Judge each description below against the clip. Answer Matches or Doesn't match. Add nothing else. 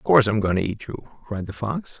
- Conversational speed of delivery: Doesn't match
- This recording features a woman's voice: Doesn't match